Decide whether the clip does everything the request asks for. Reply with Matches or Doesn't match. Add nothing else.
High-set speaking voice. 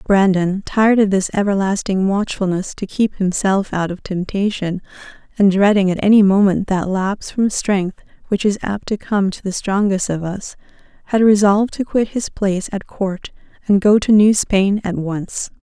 Matches